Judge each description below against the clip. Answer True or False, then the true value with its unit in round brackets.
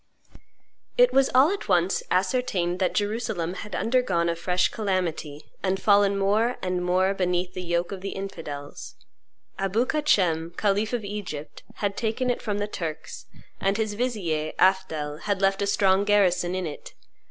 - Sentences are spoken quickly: False (160 wpm)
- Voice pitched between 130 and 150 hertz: False (195 Hz)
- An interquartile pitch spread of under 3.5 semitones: True (2.9 semitones)